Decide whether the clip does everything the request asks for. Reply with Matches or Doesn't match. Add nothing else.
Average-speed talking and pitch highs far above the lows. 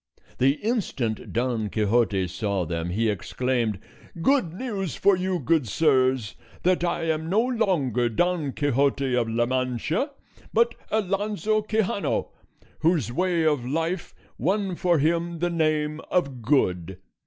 Doesn't match